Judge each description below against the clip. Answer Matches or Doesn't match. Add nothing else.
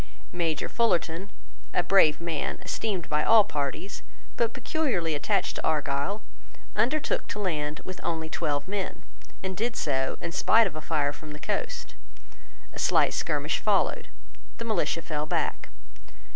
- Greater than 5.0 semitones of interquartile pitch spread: Matches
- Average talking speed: Matches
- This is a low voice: Doesn't match